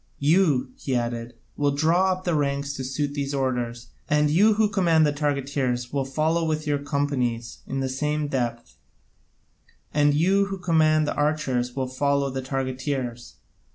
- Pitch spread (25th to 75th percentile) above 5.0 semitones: No, average, 3.0 semitones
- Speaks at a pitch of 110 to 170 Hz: Yes, medium, 140 Hz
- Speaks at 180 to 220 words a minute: No, average, 160 wpm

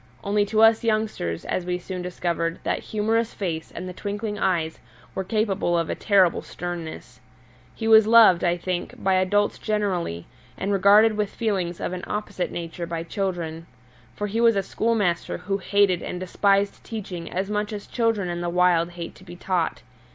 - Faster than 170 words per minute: Yes, average, 180 wpm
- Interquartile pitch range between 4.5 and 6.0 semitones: No, average, 3.2 semitones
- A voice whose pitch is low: No, high, 190 Hz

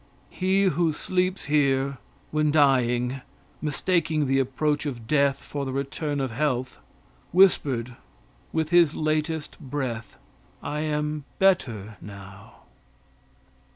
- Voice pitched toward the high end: No, medium, 145 Hz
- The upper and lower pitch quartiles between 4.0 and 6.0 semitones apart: No, average, 3.1 semitones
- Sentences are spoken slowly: Yes, slow, 110 wpm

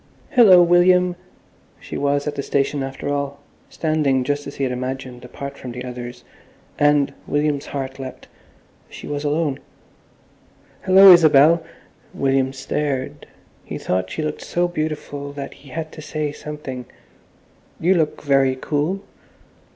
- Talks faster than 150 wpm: No, slow, 135 wpm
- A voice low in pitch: No, medium, 145 Hz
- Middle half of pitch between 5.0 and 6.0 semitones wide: No, narrow, 2.5 semitones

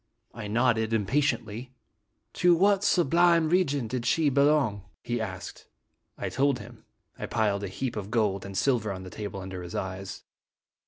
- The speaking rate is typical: Yes, average, 175 wpm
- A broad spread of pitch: Yes, wide, 5.8 semitones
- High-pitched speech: No, low, 115 Hz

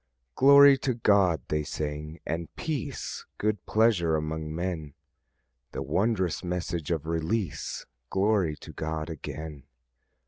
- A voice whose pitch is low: Yes, very low, 85 Hz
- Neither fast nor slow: No, slow, 115 wpm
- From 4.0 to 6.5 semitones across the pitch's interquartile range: Yes, average, 5.1 semitones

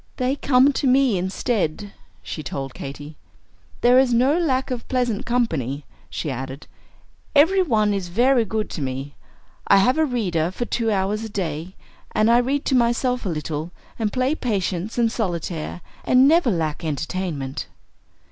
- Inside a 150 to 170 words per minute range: Yes, average, 160 wpm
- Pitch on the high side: Yes, high, 215 Hz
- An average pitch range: No, wide, 7.4 semitones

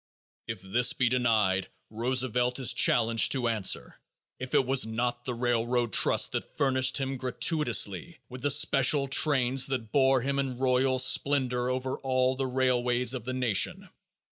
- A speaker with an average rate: Yes, average, 155 wpm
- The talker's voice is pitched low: Yes, low, 125 Hz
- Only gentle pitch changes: Yes, narrow, 1.6 semitones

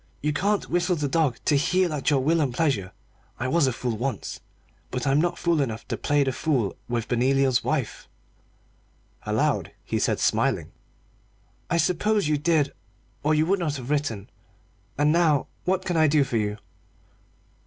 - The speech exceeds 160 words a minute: Yes, average, 175 wpm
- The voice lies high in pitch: No, medium, 145 Hz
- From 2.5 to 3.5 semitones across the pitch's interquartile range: No, average, 4.2 semitones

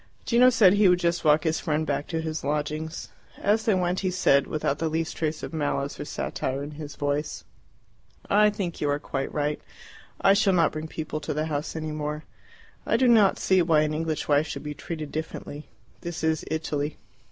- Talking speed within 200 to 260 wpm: Yes, fast, 205 wpm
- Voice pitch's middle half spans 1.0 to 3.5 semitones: Yes, average, 2.9 semitones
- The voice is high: No, medium, 155 Hz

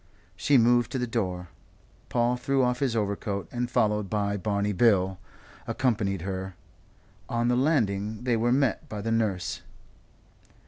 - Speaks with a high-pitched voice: No, low, 110 Hz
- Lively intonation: No, average, 3.5 semitones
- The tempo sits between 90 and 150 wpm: Yes, average, 145 wpm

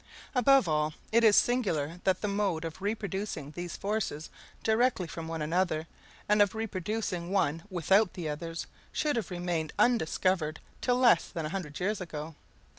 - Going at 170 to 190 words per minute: No, average, 160 wpm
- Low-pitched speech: No, medium, 185 Hz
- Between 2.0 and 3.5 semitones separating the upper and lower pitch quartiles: No, average, 4.6 semitones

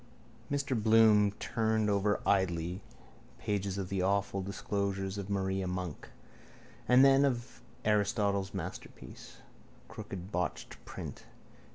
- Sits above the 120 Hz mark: No, low, 100 Hz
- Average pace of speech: No, slow, 100 wpm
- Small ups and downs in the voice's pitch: Yes, narrow, 2.2 semitones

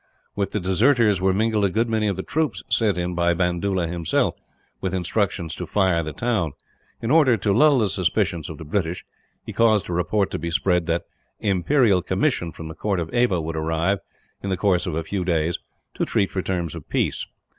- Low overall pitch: Yes, very low, 95 Hz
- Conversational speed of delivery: No, fast, 210 wpm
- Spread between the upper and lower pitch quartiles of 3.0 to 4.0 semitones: Yes, average, 3.6 semitones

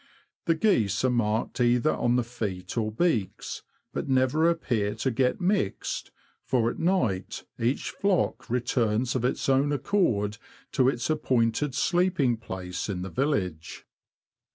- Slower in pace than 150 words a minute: Yes, average, 140 wpm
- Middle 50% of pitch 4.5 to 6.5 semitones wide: Yes, average, 5.1 semitones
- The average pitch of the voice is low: Yes, low, 125 Hz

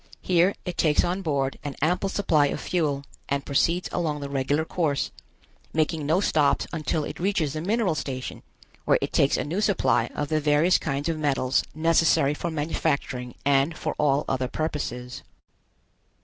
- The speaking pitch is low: No, medium, 150 Hz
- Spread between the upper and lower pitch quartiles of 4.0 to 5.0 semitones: No, average, 3.2 semitones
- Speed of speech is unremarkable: Yes, average, 165 wpm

